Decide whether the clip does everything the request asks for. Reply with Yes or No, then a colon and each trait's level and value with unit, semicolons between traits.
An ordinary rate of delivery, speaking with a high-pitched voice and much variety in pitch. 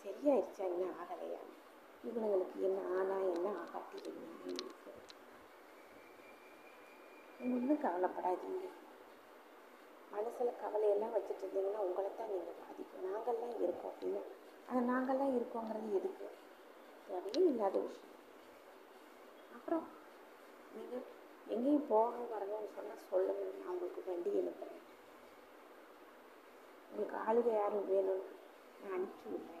Yes: average, 85 wpm; high, 220 Hz; wide, 6.5 semitones